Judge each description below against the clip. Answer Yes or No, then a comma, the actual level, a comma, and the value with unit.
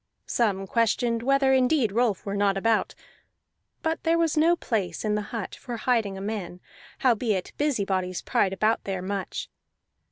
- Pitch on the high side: Yes, high, 220 Hz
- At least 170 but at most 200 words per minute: No, average, 155 wpm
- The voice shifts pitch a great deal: No, average, 4.4 semitones